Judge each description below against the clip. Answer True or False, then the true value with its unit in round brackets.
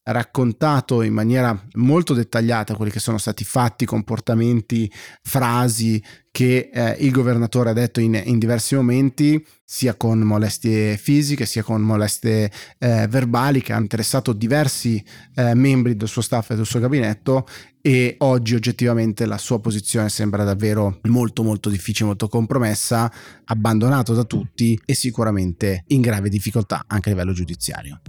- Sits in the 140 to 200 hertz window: False (115 Hz)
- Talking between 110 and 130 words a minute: False (145 wpm)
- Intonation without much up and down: True (2.2 semitones)